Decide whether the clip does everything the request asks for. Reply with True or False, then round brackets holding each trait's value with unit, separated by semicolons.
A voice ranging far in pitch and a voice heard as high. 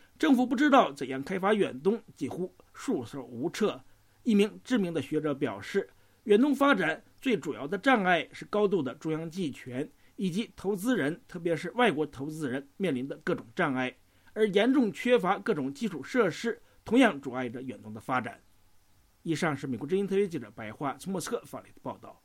False (7.8 semitones; 175 Hz)